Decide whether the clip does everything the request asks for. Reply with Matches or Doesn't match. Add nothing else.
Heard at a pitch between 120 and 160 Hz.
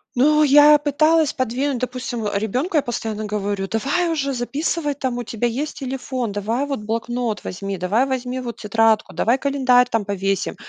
Doesn't match